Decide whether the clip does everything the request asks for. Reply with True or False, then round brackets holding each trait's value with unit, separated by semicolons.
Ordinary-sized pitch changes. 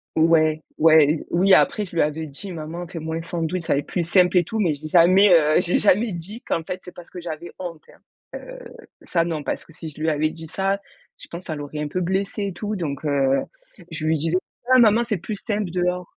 True (3.0 semitones)